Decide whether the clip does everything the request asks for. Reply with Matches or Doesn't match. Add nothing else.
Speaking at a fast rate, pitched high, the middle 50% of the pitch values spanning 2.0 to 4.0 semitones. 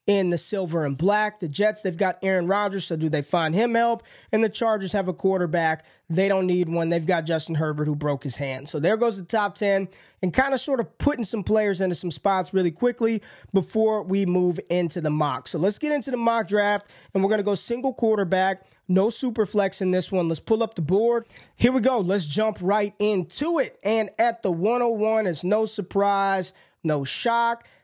Matches